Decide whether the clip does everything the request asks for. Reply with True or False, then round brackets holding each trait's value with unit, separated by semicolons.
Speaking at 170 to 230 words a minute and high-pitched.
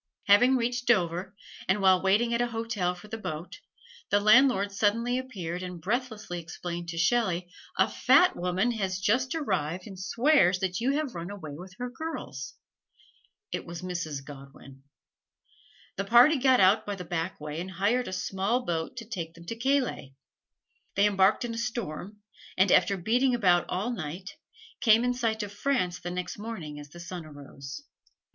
True (175 wpm; 195 Hz)